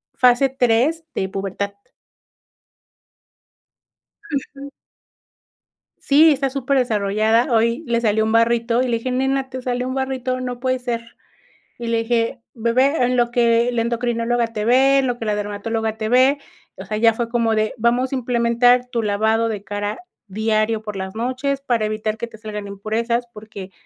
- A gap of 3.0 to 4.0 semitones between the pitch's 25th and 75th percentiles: No, narrow, 2.6 semitones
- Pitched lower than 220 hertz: No, high, 235 Hz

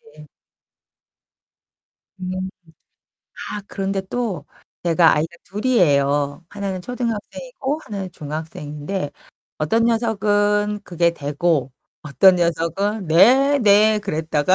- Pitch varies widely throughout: No, average, 4.8 semitones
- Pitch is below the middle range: No, medium, 185 Hz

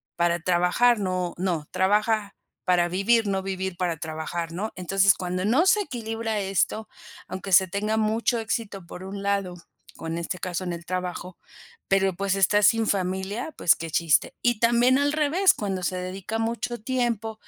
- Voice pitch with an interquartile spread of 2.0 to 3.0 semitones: No, average, 3.6 semitones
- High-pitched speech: Yes, high, 195 Hz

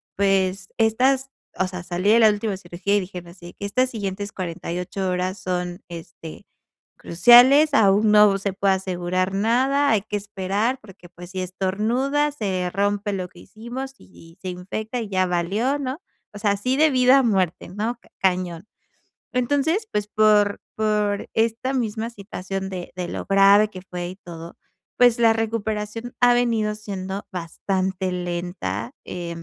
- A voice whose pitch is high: Yes, high, 200 Hz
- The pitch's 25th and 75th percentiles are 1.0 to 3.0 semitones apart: No, average, 3.5 semitones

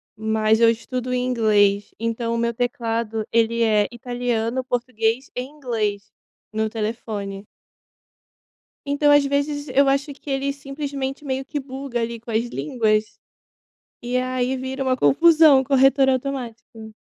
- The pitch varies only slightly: No, average, 3.2 semitones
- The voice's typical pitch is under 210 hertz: No, high, 245 Hz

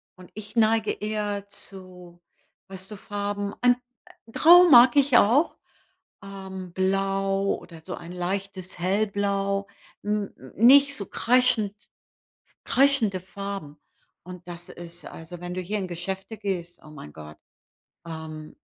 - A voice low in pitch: No, high, 195 Hz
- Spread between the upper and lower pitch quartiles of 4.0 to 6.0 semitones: No, average, 2.9 semitones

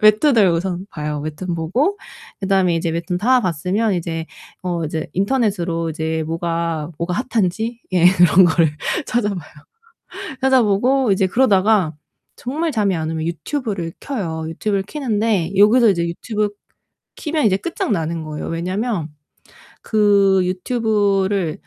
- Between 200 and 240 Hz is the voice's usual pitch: No, high, 190 Hz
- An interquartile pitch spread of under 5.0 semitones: Yes, average, 4.6 semitones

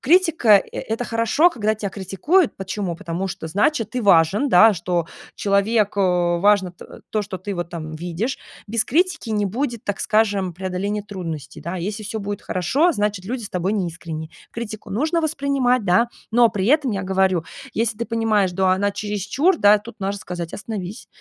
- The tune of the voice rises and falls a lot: No, average, 3.7 semitones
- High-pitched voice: Yes, high, 205 Hz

